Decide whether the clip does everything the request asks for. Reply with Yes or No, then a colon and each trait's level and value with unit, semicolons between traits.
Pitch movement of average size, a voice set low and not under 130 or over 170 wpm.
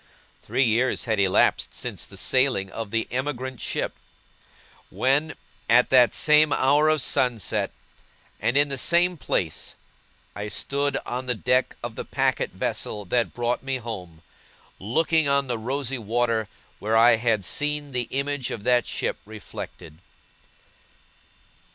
Yes: average, 3.8 semitones; low, 125 Hz; average, 140 wpm